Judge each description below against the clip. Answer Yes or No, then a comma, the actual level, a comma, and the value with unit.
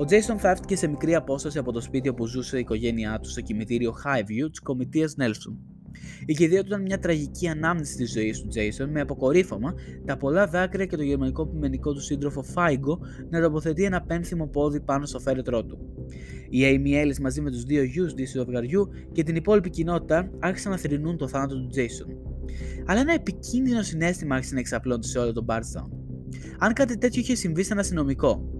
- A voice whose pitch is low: No, medium, 145 Hz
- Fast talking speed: Yes, fast, 195 wpm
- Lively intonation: Yes, wide, 5.8 semitones